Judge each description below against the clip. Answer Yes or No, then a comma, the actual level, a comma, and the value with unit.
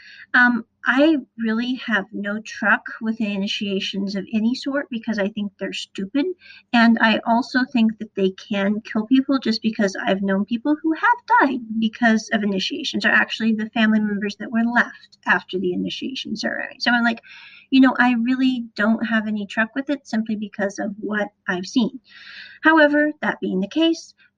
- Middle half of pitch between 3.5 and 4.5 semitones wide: Yes, average, 4.2 semitones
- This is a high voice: Yes, high, 225 Hz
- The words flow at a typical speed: Yes, average, 175 wpm